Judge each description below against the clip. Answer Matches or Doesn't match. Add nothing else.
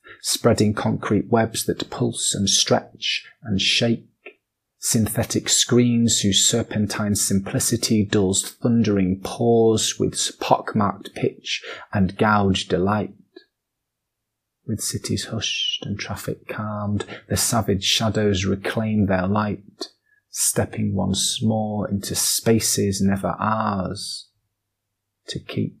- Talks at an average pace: Doesn't match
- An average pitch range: Doesn't match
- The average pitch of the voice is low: Matches